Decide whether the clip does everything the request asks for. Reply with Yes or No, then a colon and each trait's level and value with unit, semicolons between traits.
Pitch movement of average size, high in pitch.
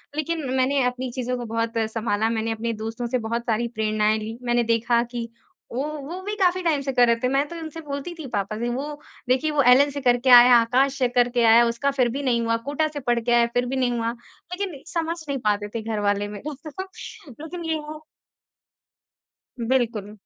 Yes: average, 3.7 semitones; high, 245 Hz